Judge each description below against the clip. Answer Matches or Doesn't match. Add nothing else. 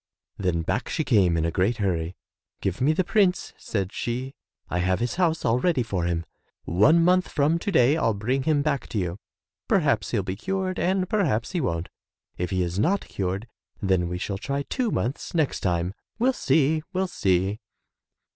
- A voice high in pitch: Doesn't match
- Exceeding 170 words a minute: Matches